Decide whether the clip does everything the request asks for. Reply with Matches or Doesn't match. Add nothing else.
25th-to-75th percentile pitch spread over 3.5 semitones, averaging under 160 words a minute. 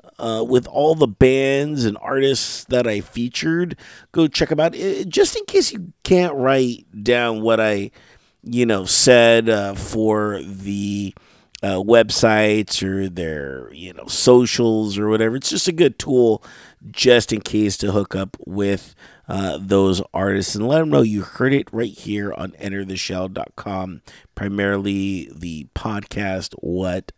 Matches